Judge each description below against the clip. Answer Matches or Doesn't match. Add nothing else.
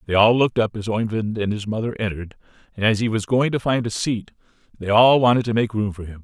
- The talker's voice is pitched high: Doesn't match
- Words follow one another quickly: Matches